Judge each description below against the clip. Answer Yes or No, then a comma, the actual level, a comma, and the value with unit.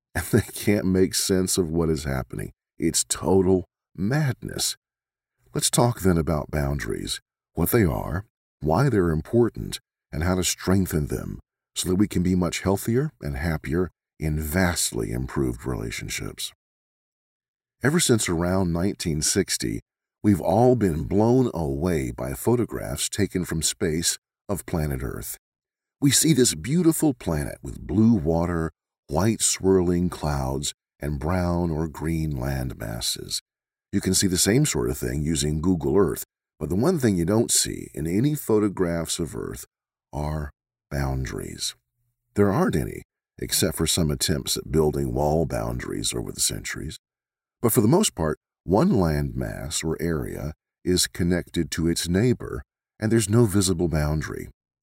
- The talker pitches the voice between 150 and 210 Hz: No, very low, 85 Hz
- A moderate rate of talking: Yes, average, 145 wpm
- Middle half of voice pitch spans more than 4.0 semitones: Yes, average, 5.1 semitones